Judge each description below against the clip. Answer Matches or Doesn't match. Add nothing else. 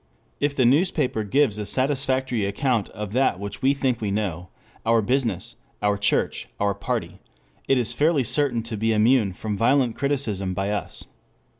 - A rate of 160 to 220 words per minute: Matches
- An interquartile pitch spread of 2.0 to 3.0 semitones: Doesn't match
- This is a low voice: Matches